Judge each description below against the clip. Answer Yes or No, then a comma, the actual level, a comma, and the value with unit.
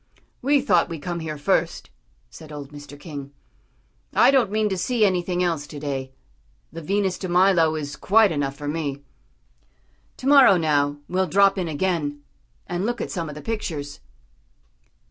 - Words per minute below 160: No, average, 165 wpm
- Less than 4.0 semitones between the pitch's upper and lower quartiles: No, average, 5.0 semitones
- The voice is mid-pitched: Yes, medium, 170 Hz